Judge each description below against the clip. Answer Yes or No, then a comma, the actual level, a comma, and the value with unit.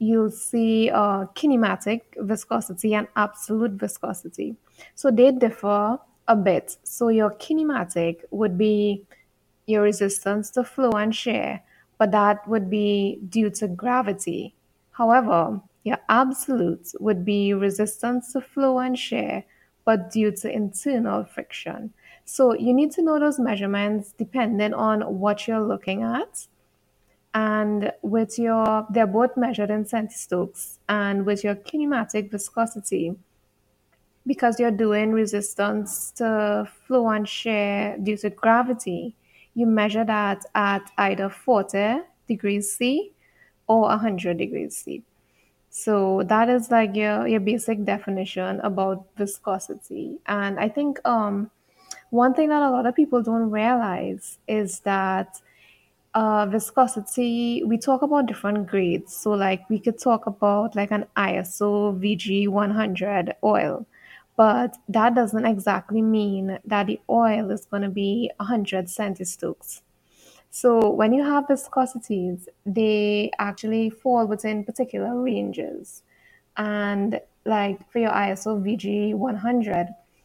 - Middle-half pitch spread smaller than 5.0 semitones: Yes, narrow, 2.5 semitones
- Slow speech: Yes, slow, 130 wpm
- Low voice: No, high, 215 Hz